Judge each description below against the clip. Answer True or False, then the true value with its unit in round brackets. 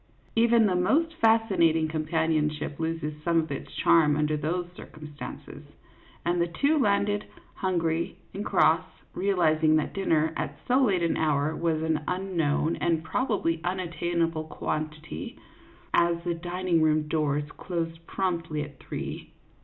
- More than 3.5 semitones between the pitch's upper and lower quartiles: False (2.9 semitones)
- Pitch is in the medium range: True (165 Hz)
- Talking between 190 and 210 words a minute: False (145 wpm)